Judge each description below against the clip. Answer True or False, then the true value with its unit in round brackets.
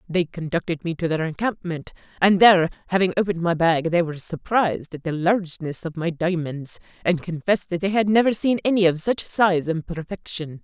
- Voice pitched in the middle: True (175 Hz)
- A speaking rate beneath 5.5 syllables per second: False (5.6 syllables/s)